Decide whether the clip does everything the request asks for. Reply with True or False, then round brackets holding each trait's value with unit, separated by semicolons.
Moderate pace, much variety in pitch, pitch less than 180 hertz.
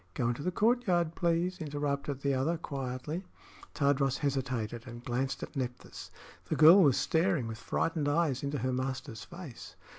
False (155 wpm; 4.4 semitones; 140 Hz)